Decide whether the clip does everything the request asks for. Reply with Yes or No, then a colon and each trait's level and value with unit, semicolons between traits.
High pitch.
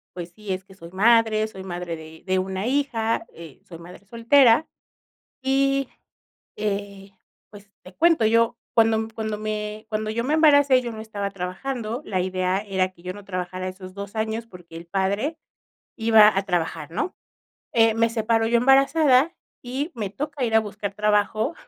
Yes: high, 215 Hz